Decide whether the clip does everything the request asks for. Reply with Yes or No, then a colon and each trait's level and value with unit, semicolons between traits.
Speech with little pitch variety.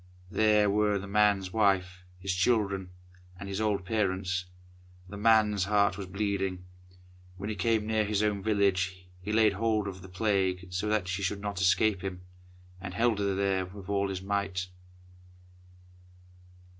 Yes: narrow, 2.1 semitones